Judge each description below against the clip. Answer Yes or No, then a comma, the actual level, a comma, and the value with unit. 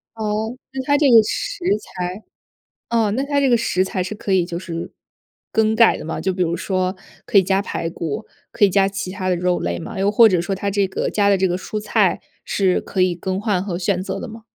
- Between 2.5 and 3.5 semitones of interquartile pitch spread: Yes, average, 3.0 semitones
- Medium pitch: No, high, 195 Hz